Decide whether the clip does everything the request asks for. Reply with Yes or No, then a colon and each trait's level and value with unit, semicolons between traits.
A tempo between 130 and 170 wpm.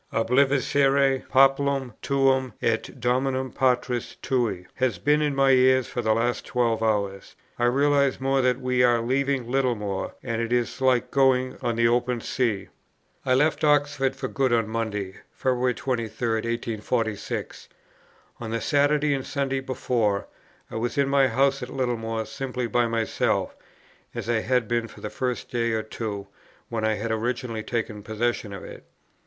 Yes: average, 160 wpm